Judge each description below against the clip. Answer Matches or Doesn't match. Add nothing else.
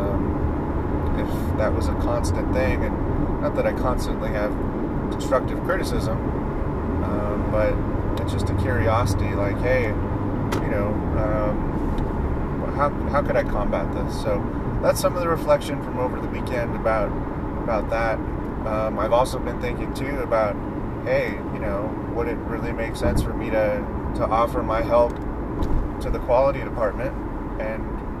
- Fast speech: Doesn't match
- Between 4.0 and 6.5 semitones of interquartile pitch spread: Matches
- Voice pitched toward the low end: Matches